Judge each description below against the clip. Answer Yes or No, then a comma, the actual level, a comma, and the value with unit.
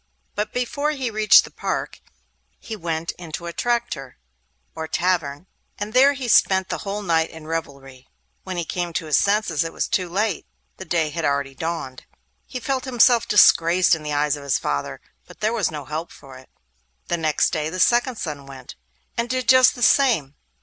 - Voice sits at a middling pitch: Yes, medium, 170 Hz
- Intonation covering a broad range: Yes, wide, 6.5 semitones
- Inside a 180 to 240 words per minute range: Yes, average, 190 wpm